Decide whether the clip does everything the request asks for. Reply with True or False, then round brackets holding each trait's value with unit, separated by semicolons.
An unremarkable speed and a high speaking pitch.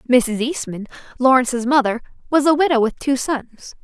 True (155 wpm; 255 Hz)